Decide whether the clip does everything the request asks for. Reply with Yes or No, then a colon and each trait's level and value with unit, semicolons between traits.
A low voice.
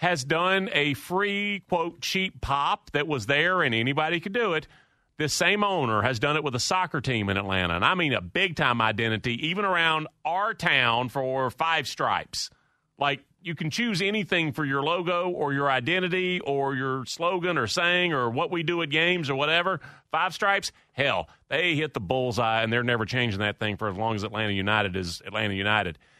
No: medium, 145 Hz